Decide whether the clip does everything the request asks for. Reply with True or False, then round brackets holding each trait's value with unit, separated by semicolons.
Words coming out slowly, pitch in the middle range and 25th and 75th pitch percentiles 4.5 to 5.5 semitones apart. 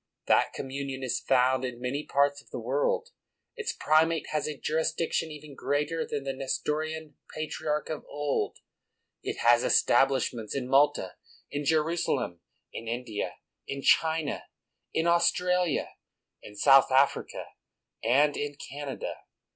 False (130 wpm; 145 Hz; 2.8 semitones)